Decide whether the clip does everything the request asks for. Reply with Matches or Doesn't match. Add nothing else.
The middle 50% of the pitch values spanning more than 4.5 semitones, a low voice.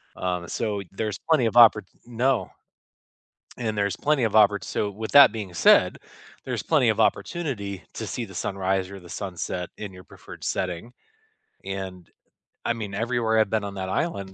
Doesn't match